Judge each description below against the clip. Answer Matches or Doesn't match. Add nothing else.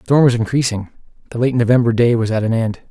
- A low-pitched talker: Matches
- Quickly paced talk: Matches